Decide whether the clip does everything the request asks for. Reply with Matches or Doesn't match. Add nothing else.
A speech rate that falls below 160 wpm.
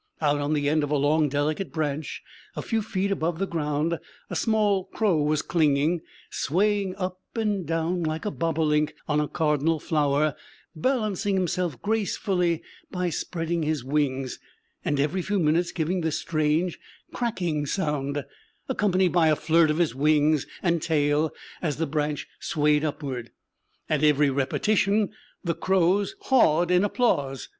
Matches